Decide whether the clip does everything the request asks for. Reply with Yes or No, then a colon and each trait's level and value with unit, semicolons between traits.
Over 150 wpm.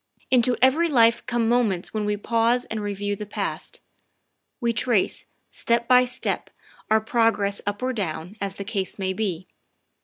Yes: average, 165 wpm